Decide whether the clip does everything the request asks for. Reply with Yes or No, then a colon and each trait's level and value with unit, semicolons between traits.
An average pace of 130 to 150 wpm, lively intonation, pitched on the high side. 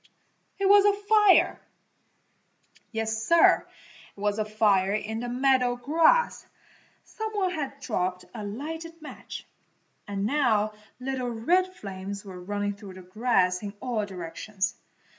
Yes: slow, 135 wpm; wide, 7.3 semitones; high, 225 Hz